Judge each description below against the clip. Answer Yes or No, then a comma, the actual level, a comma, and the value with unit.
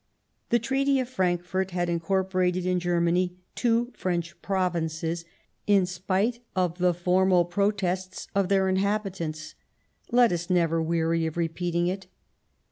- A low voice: No, medium, 180 Hz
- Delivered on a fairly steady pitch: Yes, narrow, 2.1 semitones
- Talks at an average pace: No, slow, 125 wpm